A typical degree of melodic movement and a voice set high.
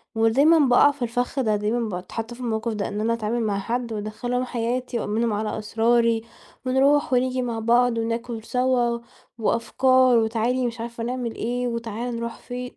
No: narrow, 1.8 semitones; high, 235 Hz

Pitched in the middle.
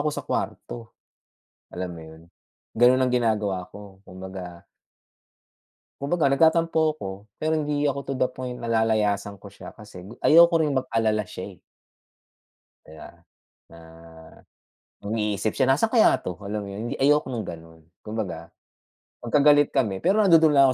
No: low, 115 Hz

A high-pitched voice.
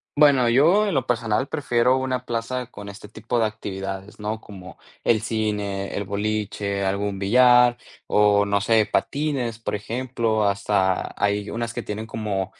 No: low, 110 Hz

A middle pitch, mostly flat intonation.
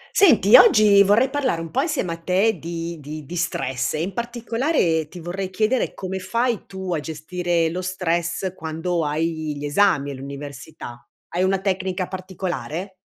No: medium, 180 Hz; average, 3.5 semitones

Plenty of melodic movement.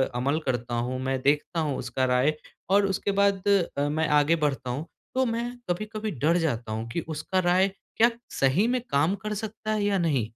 Yes: wide, 7.5 semitones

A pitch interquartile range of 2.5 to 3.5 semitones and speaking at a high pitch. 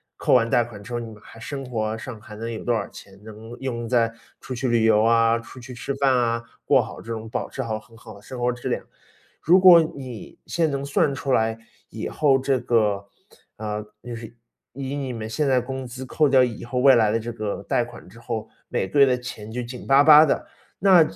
No: average, 2.9 semitones; low, 120 Hz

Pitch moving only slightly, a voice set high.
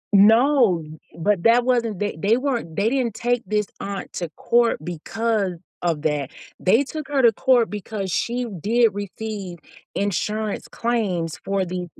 No: average, 4.1 semitones; high, 215 Hz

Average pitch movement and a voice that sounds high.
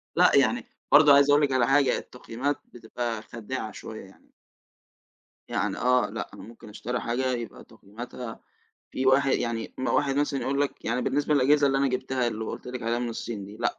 No: average, 3.0 semitones; low, 125 Hz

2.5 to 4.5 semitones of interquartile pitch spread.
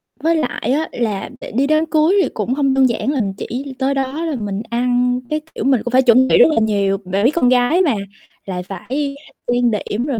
Yes: average, 4.0 semitones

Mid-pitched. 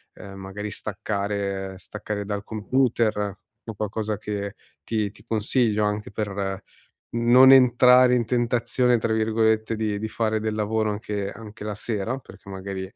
No: low, 110 Hz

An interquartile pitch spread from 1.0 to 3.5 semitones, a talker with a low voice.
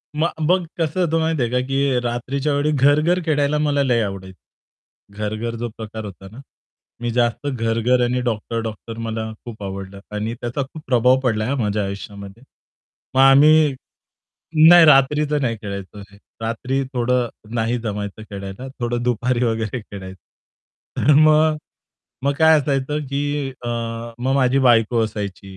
No: average, 4.1 semitones; low, 120 Hz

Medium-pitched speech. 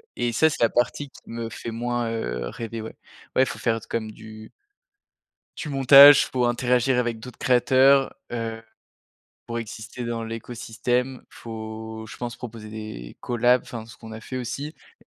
No: low, 115 Hz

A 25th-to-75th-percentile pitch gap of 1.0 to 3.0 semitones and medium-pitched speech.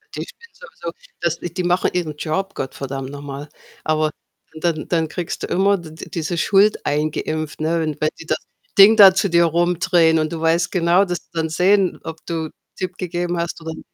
Yes: narrow, 2.5 semitones; medium, 170 Hz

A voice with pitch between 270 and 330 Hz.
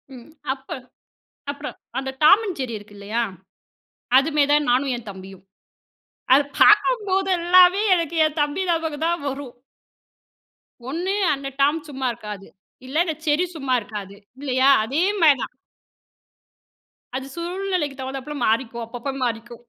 Yes: very high, 280 Hz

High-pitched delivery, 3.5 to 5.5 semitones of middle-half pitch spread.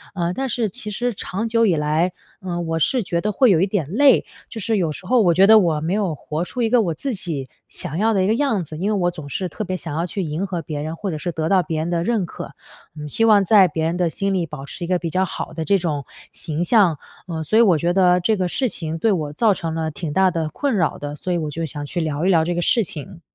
No: medium, 175 Hz; average, 4.1 semitones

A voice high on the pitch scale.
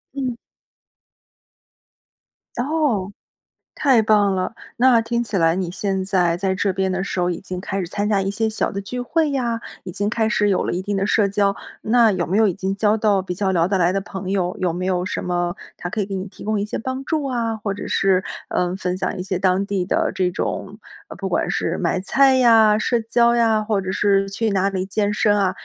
Yes: high, 200 Hz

